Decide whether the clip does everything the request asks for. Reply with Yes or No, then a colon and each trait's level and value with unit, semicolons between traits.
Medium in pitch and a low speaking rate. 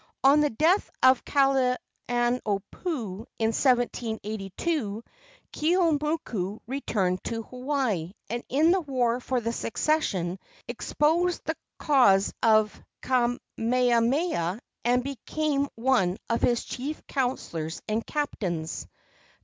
No: high, 245 Hz; slow, 100 wpm